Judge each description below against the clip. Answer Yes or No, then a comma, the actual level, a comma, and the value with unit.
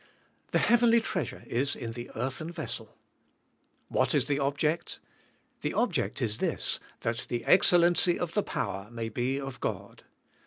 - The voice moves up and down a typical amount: No, wide, 6.4 semitones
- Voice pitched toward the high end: No, low, 135 Hz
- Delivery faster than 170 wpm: No, average, 155 wpm